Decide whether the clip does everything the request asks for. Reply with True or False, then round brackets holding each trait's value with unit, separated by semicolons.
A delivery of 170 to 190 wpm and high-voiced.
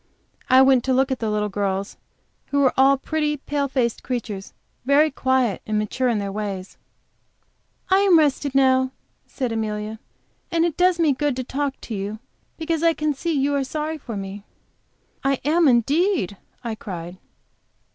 True (175 wpm; 260 Hz)